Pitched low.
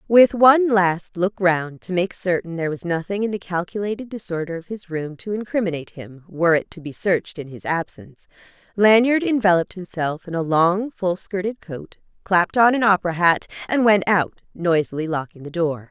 No: medium, 185 Hz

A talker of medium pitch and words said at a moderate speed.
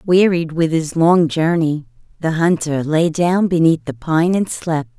Yes: medium, 160 Hz; average, 170 wpm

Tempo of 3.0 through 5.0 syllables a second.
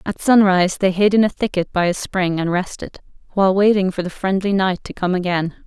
No: 5.6 syllables/s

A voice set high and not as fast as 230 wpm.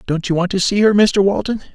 No: high, 195 Hz; fast, 275 wpm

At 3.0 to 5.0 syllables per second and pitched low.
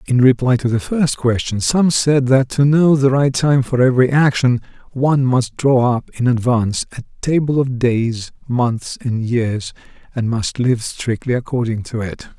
Yes: 4.5 syllables/s; low, 125 Hz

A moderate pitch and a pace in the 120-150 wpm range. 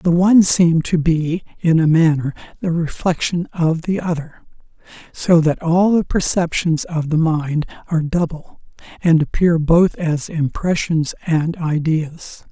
Yes: medium, 165 Hz; average, 145 wpm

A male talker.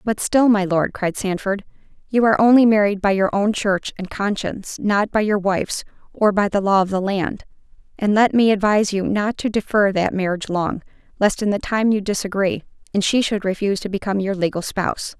No: female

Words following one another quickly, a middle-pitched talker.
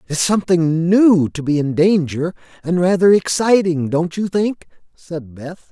No: average, 155 wpm; medium, 170 Hz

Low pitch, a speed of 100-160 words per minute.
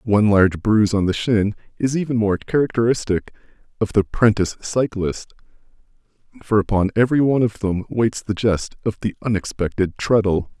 Yes: low, 105 Hz; average, 155 wpm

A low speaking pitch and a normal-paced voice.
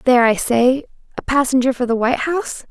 No: very high, 255 Hz; average, 155 wpm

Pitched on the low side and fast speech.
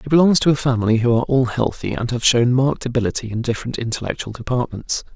Yes: low, 125 Hz; fast, 210 wpm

